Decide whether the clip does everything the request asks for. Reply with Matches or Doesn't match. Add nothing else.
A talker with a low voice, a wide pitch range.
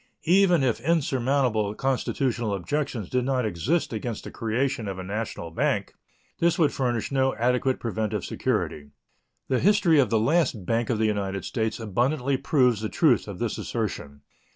Doesn't match